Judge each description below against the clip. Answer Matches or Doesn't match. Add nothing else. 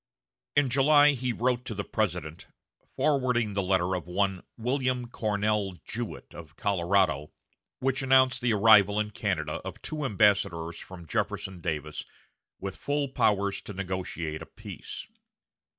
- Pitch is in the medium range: Doesn't match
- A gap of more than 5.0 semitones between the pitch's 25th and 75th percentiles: Matches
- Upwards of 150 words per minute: Doesn't match